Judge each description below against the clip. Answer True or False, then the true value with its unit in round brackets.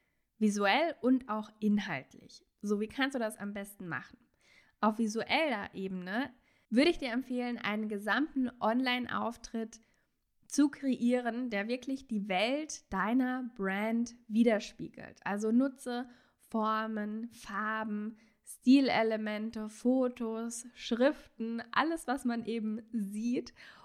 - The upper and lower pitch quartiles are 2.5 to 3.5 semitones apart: True (2.8 semitones)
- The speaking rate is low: True (110 wpm)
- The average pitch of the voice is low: False (230 Hz)